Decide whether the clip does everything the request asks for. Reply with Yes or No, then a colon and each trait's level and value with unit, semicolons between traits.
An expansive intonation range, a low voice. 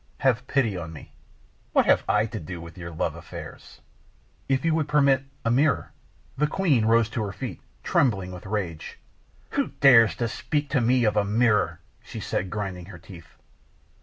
Yes: wide, 6.0 semitones; low, 110 Hz